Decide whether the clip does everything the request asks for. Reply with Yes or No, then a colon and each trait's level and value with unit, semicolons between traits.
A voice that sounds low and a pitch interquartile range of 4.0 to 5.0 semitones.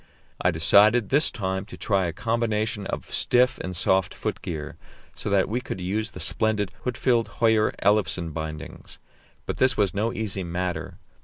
No: low, 100 Hz; average, 3.6 semitones